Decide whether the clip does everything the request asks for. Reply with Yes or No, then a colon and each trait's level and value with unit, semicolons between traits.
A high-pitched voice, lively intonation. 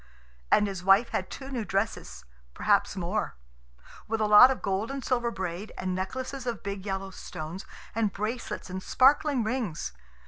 No: high, 210 Hz; average, 4.4 semitones